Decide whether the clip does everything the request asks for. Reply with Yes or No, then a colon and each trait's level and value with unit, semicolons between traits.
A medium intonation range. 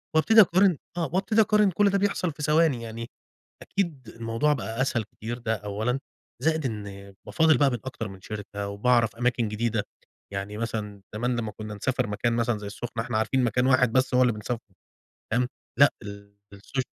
Yes: average, 4.9 semitones